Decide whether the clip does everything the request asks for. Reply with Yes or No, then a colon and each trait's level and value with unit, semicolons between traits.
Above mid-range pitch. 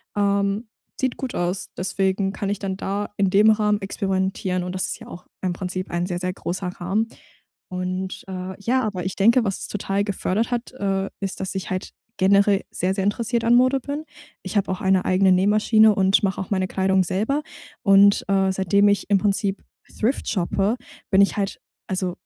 Yes: high, 195 Hz